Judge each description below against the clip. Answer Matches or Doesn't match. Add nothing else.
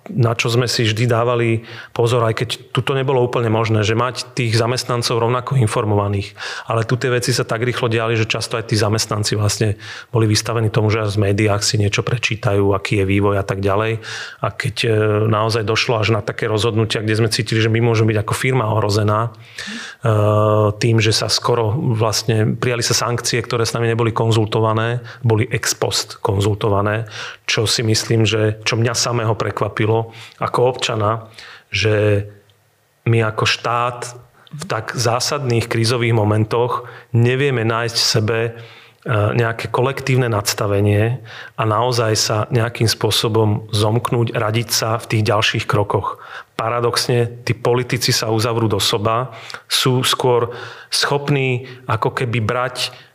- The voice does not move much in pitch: Matches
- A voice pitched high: Doesn't match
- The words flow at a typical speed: Matches